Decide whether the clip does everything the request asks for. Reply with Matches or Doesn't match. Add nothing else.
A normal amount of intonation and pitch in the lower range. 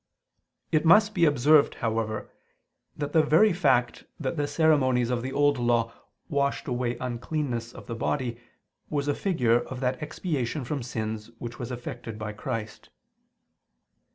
Matches